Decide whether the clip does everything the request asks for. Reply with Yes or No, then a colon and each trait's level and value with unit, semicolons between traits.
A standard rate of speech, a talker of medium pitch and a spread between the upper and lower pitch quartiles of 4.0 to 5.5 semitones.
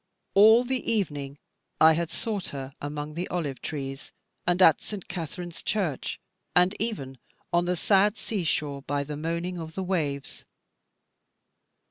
Yes: average, 145 wpm; medium, 170 Hz; average, 4.7 semitones